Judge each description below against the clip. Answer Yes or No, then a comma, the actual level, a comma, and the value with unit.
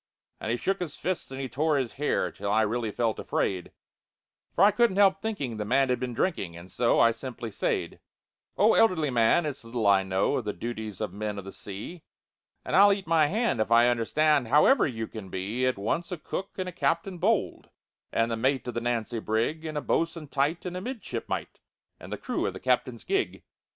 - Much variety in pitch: Yes, wide, 7.4 semitones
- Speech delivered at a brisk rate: Yes, fast, 220 wpm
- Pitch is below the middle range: Yes, low, 130 Hz